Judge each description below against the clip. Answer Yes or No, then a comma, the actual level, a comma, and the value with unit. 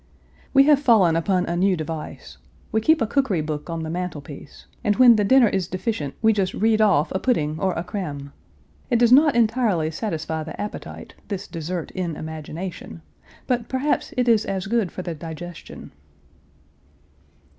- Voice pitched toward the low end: No, medium, 185 Hz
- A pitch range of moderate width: No, wide, 6.0 semitones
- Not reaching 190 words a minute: Yes, average, 170 wpm